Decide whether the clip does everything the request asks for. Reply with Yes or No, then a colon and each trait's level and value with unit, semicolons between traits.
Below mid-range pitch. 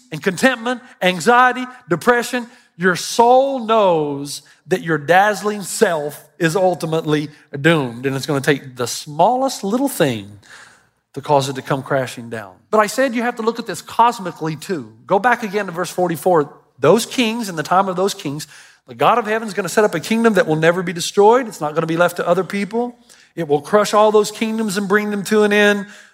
No: high, 190 Hz